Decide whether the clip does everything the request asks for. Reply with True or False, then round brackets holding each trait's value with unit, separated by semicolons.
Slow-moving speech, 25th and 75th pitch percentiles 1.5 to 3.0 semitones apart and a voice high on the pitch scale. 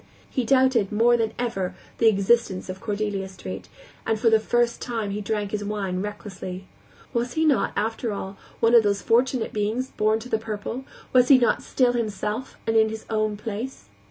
False (185 wpm; 2.6 semitones; 220 Hz)